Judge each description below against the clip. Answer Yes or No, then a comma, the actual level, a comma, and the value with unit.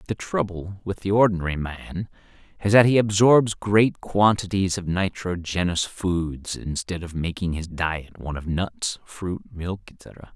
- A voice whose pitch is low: Yes, very low, 95 Hz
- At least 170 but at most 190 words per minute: No, average, 150 wpm